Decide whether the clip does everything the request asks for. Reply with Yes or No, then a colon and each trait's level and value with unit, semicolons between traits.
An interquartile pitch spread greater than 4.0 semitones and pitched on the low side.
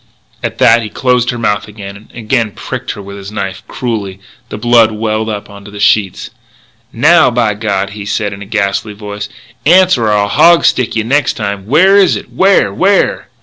No: average, 3.3 semitones; low, 110 Hz